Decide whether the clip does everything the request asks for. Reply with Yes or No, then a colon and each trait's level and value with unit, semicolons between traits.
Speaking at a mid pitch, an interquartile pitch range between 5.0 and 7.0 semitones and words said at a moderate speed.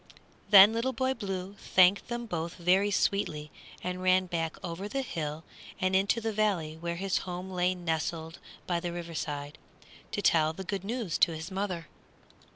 No: medium, 180 Hz; average, 3.3 semitones; average, 170 wpm